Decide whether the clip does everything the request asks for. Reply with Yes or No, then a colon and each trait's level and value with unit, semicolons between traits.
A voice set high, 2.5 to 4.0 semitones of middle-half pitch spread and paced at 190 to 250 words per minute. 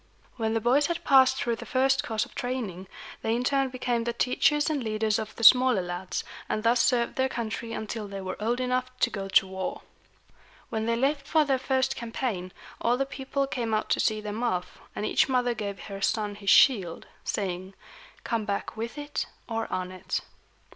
Yes: high, 230 Hz; average, 3.6 semitones; average, 200 wpm